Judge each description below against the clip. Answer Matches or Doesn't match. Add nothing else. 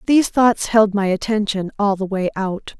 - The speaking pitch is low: Doesn't match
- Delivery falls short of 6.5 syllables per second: Matches